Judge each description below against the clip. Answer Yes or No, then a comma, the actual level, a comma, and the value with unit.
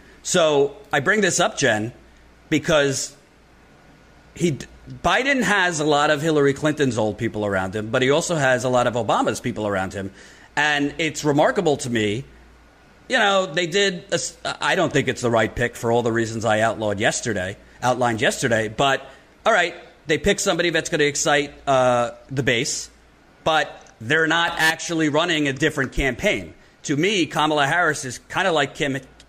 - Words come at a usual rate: Yes, average, 175 wpm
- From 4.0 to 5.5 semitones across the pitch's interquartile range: Yes, average, 4.7 semitones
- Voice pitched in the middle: Yes, medium, 145 Hz